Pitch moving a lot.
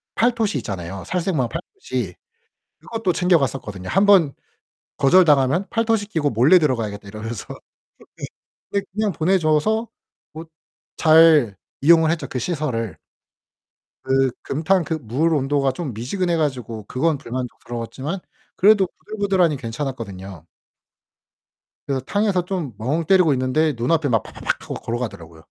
Yes: wide, 6.9 semitones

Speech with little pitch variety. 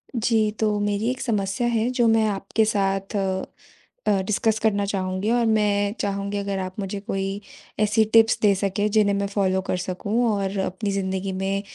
Yes: narrow, 2.0 semitones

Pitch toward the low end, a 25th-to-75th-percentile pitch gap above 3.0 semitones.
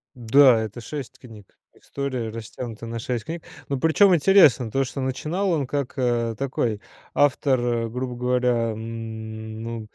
Yes: low, 125 Hz; average, 3.4 semitones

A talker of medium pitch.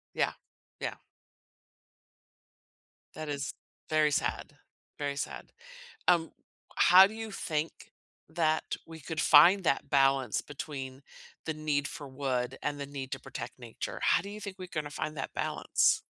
Yes: medium, 150 Hz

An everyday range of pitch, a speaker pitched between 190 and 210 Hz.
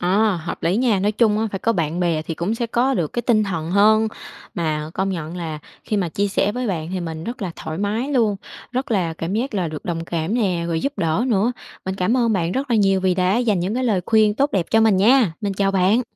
Yes: average, 4.6 semitones; high, 195 Hz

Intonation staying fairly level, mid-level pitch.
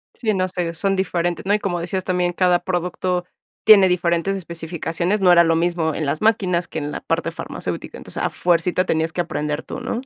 Yes: narrow, 1.9 semitones; medium, 175 Hz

